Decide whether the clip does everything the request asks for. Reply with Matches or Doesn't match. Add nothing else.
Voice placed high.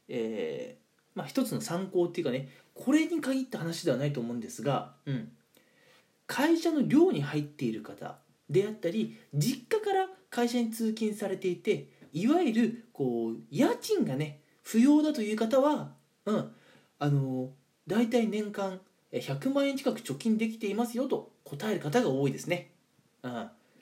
Matches